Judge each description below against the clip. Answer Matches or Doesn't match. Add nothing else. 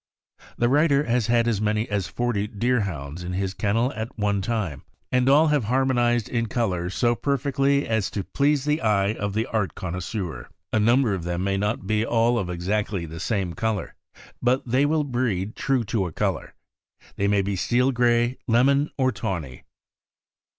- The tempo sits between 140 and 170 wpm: Doesn't match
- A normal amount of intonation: Matches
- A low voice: Matches